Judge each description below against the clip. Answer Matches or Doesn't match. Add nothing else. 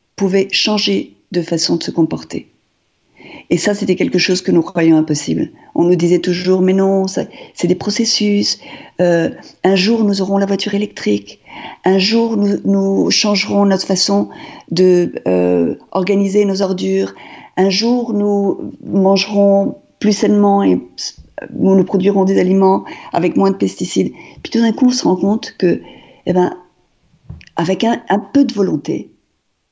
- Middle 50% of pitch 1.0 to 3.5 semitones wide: Matches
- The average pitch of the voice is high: Matches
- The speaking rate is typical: Matches